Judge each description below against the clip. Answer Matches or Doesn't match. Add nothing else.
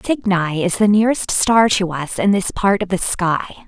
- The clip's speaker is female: Matches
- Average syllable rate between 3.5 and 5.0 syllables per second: Matches